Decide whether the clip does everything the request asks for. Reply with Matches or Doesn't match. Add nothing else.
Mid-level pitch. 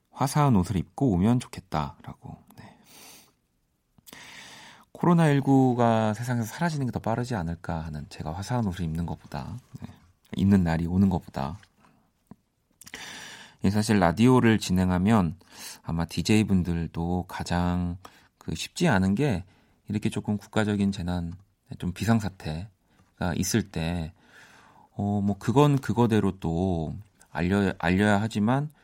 Doesn't match